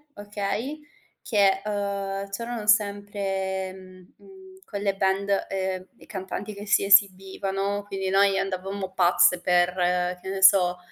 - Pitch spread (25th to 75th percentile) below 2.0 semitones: Yes, narrow, 1.1 semitones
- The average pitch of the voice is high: Yes, high, 195 Hz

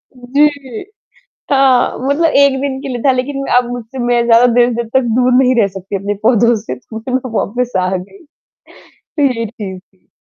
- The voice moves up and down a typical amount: Yes, average, 3.0 semitones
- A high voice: Yes, high, 245 Hz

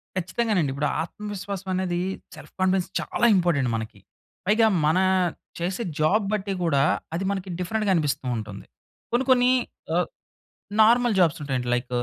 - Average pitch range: No, wide, 5.9 semitones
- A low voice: No, medium, 185 Hz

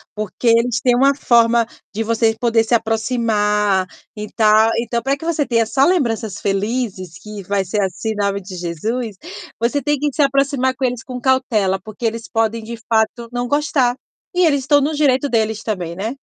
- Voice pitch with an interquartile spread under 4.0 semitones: Yes, average, 3.3 semitones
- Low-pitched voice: No, high, 230 Hz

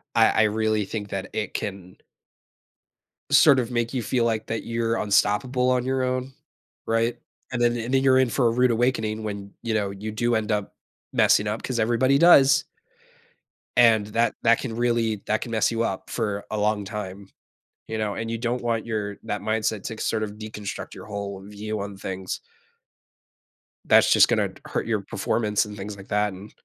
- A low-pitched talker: Yes, low, 110 Hz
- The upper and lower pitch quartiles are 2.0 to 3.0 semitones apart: Yes, narrow, 2.4 semitones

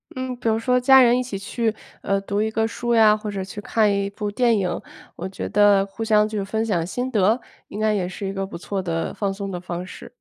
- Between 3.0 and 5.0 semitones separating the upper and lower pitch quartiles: No, narrow, 2.5 semitones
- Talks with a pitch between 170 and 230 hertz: Yes, high, 210 Hz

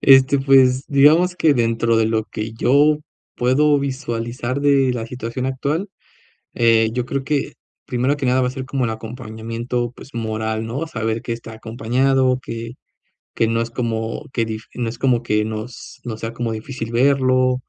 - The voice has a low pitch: Yes, low, 120 Hz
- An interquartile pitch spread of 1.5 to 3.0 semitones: Yes, average, 2.7 semitones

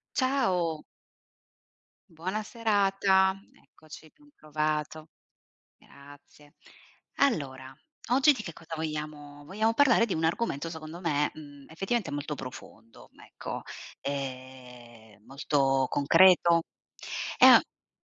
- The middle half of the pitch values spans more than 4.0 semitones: Yes, average, 5.2 semitones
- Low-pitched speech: No, medium, 155 Hz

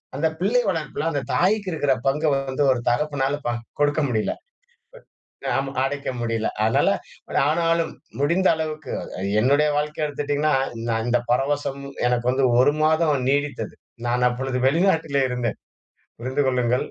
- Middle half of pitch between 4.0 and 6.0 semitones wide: No, average, 3.3 semitones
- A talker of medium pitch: Yes, medium, 145 Hz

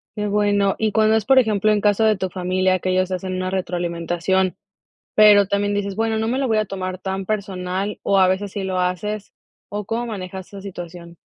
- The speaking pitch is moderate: No, high, 195 Hz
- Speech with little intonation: Yes, narrow, 2.1 semitones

